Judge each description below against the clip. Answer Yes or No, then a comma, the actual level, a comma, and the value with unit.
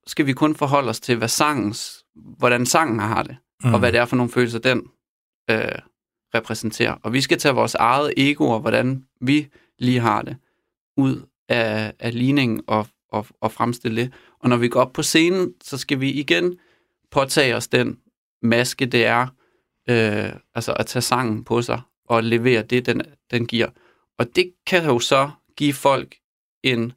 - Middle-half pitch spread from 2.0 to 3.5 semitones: Yes, average, 3.1 semitones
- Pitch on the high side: No, low, 125 Hz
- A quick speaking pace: No, average, 180 wpm